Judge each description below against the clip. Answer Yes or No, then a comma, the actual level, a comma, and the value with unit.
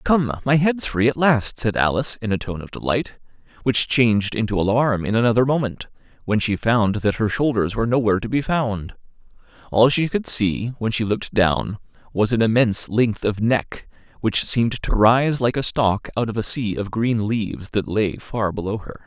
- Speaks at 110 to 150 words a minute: No, average, 200 wpm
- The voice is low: Yes, low, 115 Hz